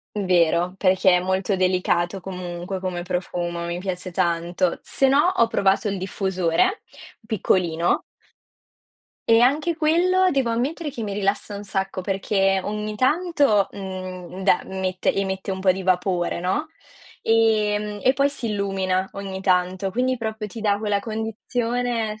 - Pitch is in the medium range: No, high, 195 Hz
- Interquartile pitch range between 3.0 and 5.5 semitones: Yes, average, 3.4 semitones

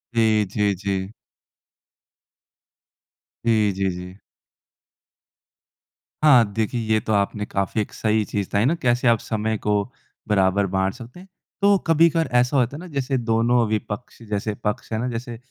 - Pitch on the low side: Yes, low, 110 Hz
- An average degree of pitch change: Yes, average, 3.2 semitones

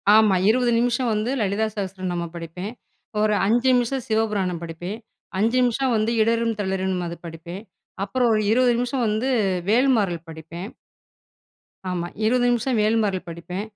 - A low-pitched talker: No, high, 215 Hz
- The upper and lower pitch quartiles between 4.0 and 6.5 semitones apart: Yes, average, 4.6 semitones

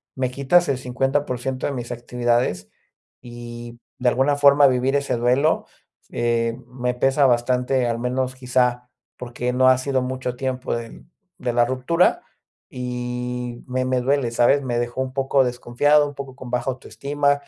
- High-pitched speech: No, low, 125 Hz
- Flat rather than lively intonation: Yes, narrow, 1.6 semitones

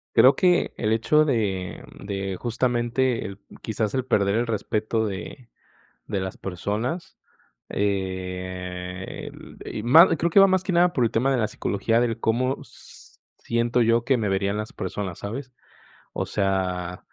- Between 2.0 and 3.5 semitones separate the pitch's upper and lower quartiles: No, average, 4.5 semitones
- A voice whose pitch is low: Yes, low, 110 Hz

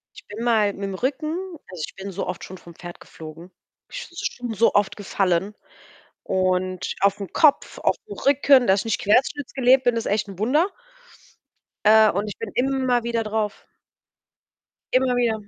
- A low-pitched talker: No, high, 215 Hz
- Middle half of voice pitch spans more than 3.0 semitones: Yes, average, 4.4 semitones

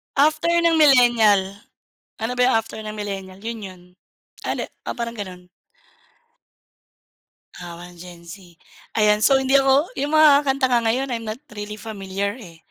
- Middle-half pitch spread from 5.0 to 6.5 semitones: Yes, wide, 5.5 semitones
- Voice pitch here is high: Yes, high, 225 Hz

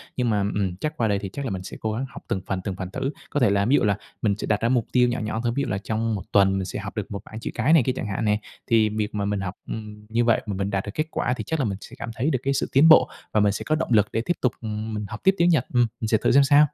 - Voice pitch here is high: No, low, 110 Hz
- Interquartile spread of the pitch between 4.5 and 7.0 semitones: No, average, 3.8 semitones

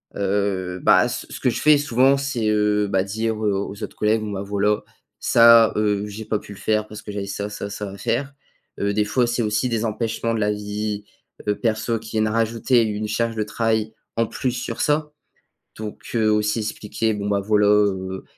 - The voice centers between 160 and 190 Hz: No, low, 105 Hz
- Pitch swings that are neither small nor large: No, narrow, 1.8 semitones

